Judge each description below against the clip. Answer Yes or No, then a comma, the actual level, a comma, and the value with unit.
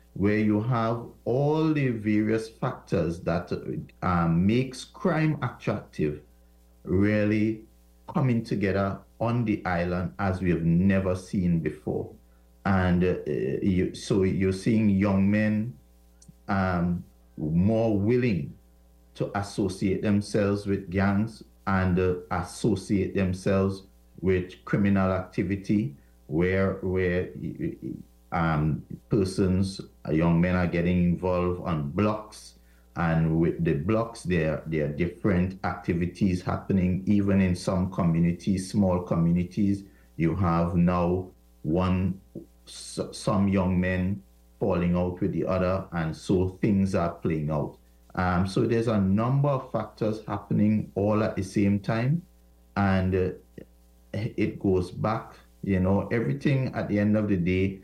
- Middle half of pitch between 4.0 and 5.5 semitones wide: No, average, 3.4 semitones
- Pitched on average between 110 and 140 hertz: No, very low, 95 Hz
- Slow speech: Yes, slow, 125 wpm